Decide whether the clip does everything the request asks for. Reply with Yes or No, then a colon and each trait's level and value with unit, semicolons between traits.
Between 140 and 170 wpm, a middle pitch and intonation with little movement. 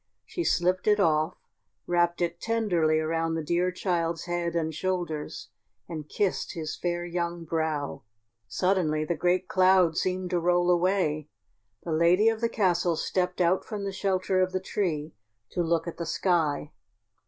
Yes: average, 160 wpm; medium, 175 Hz; narrow, 2.2 semitones